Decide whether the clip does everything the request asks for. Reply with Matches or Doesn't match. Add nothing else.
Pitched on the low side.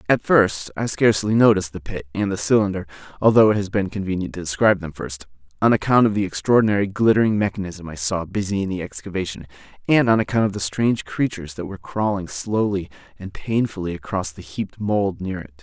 Matches